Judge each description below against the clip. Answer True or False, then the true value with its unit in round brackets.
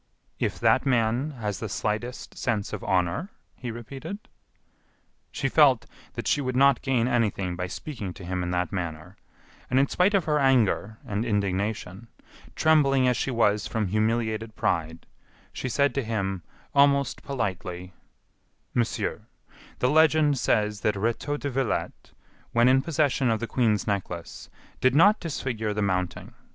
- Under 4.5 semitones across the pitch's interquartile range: False (5.2 semitones)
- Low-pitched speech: True (115 Hz)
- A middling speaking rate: True (150 wpm)